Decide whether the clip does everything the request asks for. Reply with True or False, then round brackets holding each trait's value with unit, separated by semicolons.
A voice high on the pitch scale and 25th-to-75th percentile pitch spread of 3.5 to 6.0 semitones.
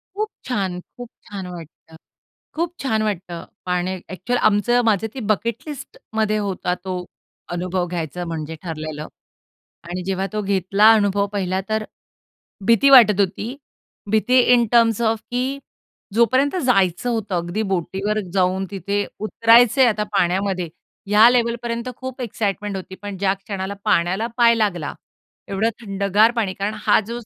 True (205 Hz; 3.8 semitones)